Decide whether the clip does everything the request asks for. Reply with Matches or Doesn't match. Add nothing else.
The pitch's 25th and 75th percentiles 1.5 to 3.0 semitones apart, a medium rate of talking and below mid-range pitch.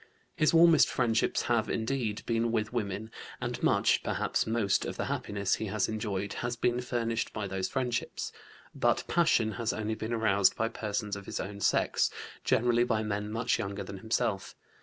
Matches